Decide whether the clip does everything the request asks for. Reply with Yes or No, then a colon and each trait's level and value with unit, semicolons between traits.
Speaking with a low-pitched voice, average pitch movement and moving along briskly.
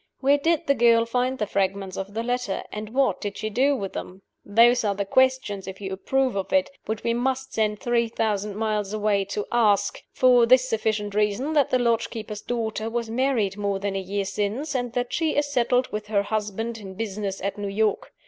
No: high, 220 Hz; average, 3.5 semitones; fast, 215 wpm